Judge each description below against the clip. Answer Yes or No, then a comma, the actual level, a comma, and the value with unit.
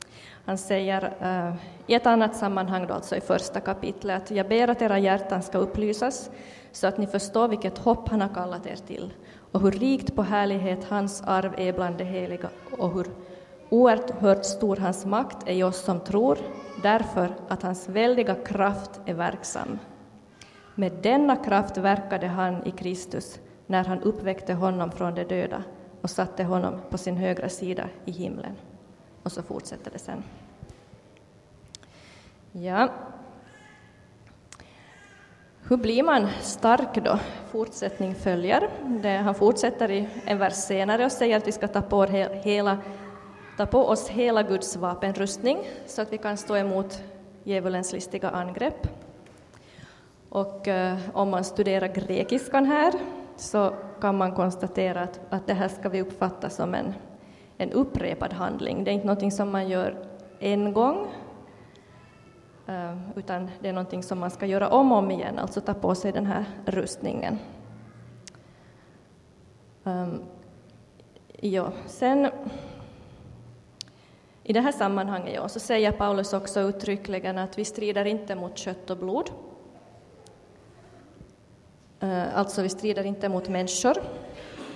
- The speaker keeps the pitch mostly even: Yes, narrow, 2.2 semitones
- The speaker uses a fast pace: No, average, 145 wpm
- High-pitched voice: Yes, high, 195 Hz